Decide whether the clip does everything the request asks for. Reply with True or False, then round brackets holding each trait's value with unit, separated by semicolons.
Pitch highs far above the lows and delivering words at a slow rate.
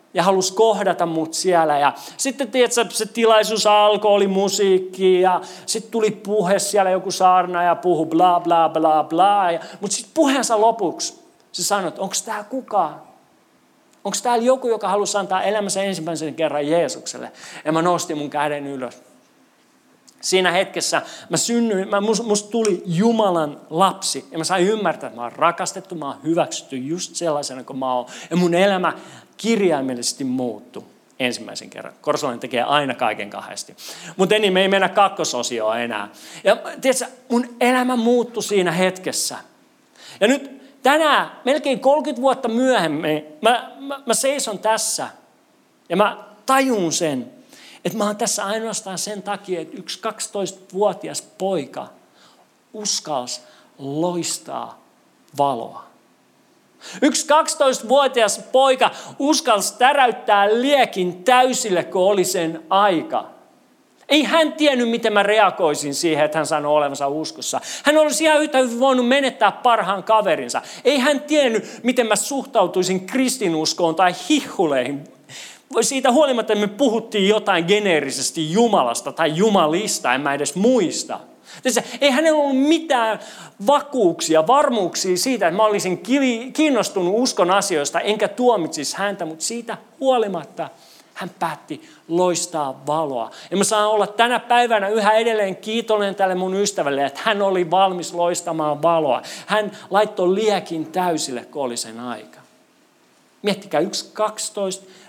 False (5.8 semitones; 140 wpm)